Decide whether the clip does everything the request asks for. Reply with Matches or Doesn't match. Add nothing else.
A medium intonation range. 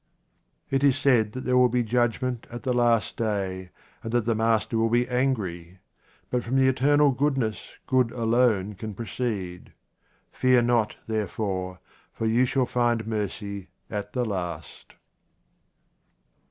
Matches